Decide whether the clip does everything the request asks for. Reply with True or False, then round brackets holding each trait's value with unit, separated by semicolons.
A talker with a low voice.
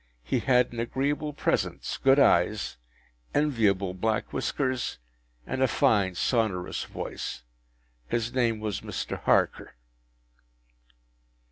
True (115 Hz)